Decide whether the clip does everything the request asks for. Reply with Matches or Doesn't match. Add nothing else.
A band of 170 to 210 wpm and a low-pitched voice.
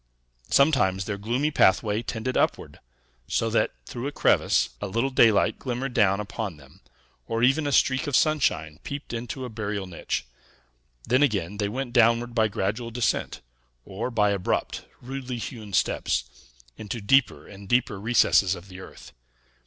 Doesn't match